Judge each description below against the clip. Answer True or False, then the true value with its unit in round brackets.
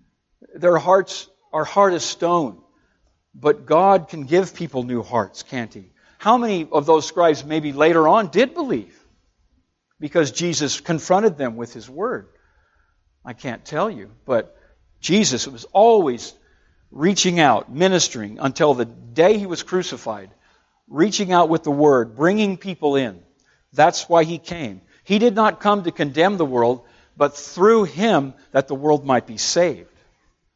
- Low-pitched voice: False (160 Hz)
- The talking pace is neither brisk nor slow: True (155 wpm)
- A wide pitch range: True (6.0 semitones)